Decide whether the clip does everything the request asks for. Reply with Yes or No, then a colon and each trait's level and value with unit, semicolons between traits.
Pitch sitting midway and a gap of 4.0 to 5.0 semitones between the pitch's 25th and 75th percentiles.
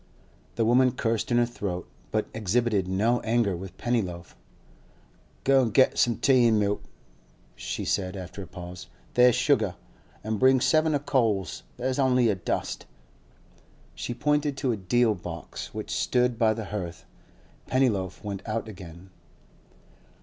No: low, 115 Hz; average, 4.4 semitones